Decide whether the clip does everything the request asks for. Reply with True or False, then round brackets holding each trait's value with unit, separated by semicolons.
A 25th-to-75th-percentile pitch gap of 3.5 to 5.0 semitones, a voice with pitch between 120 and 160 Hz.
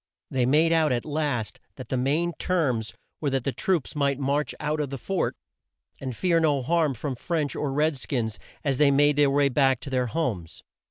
False (3.0 semitones; 140 Hz)